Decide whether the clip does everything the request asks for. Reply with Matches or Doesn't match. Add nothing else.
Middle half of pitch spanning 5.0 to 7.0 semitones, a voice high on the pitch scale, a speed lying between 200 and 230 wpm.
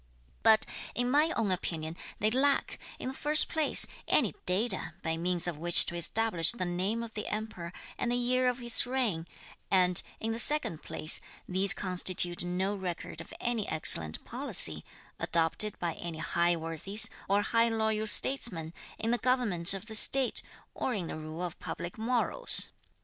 Doesn't match